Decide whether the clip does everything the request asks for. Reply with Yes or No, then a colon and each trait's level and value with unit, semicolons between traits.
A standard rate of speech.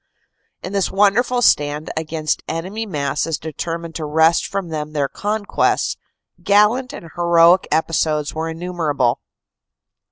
No: slow, 120 wpm